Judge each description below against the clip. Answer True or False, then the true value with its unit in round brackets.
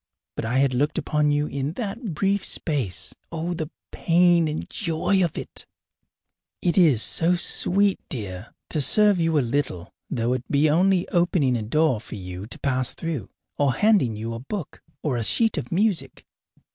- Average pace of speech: True (180 wpm)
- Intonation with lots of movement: True (6.1 semitones)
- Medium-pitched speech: True (150 Hz)